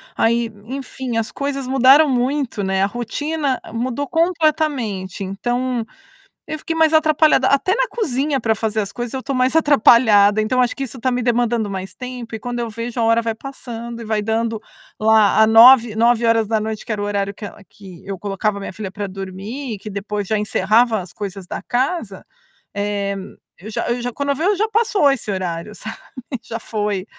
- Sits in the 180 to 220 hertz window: No, high, 230 Hz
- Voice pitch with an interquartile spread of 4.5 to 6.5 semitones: No, average, 4.0 semitones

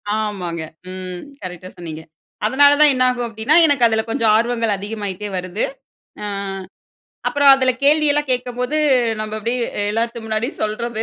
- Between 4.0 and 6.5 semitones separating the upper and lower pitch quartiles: No, average, 3.5 semitones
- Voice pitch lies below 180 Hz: No, high, 225 Hz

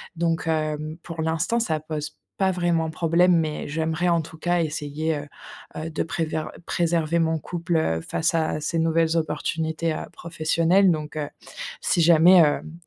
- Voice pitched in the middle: Yes, medium, 160 Hz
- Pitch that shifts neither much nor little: No, narrow, 1.3 semitones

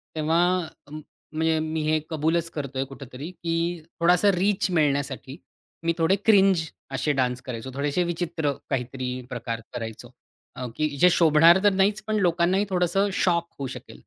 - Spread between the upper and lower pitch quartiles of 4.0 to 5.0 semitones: Yes, average, 4.4 semitones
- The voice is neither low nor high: Yes, medium, 160 Hz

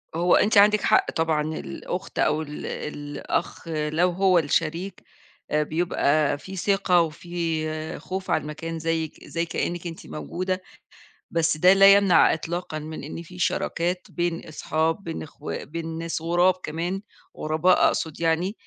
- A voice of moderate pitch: Yes, medium, 165 Hz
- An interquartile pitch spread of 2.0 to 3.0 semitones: Yes, narrow, 2.4 semitones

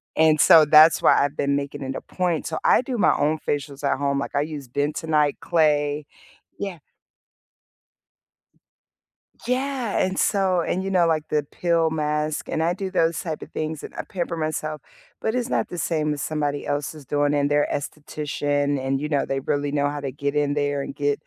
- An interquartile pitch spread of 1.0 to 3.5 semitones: Yes, narrow, 2.4 semitones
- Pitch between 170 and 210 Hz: No, medium, 150 Hz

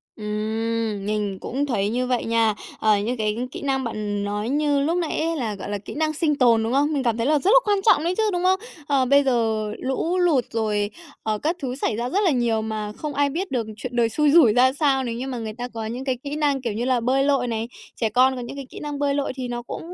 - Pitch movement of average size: Yes, average, 4.3 semitones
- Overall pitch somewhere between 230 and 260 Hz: Yes, very high, 250 Hz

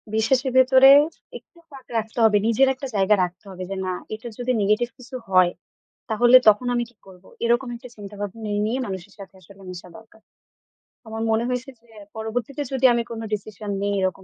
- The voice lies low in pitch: No, high, 220 Hz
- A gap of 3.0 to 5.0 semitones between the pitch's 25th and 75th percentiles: Yes, average, 3.7 semitones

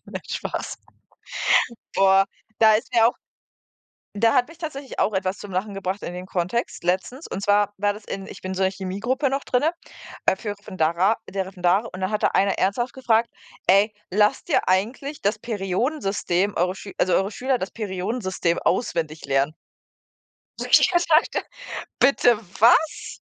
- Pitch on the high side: Yes, high, 200 Hz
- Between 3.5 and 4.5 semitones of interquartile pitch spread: Yes, average, 3.8 semitones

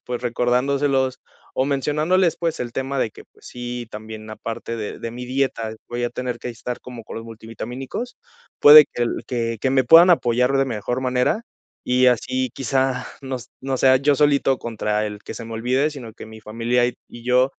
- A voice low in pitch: Yes, low, 125 Hz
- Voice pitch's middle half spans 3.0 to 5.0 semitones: No, narrow, 2.6 semitones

